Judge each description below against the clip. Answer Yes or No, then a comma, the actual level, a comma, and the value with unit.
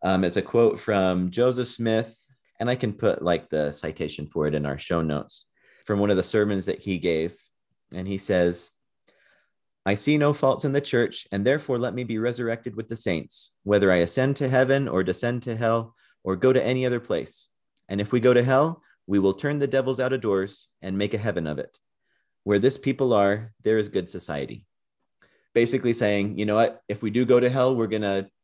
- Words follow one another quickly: Yes, fast, 215 wpm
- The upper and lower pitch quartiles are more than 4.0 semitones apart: Yes, average, 4.5 semitones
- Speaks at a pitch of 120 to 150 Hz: No, low, 110 Hz